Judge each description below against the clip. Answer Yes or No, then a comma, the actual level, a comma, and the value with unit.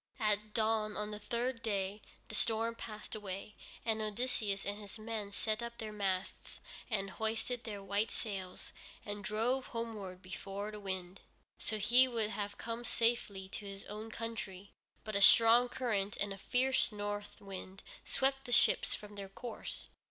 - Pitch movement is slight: Yes, narrow, 2.3 semitones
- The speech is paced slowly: No, average, 165 wpm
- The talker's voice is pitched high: Yes, high, 215 Hz